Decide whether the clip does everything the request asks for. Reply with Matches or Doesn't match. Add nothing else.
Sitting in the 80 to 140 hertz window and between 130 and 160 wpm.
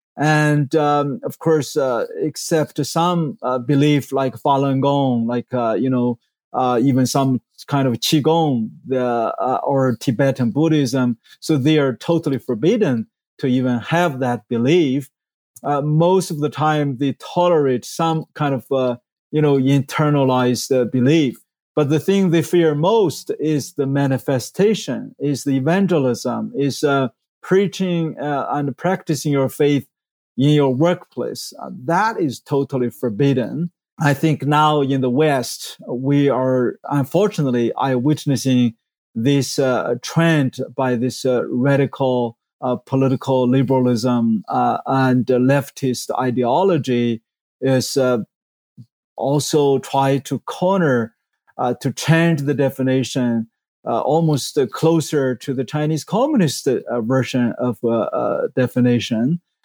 Matches